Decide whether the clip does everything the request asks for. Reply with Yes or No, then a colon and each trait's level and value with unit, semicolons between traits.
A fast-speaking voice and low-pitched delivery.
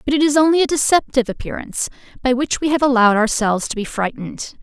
No: fast, 210 wpm; very high, 260 Hz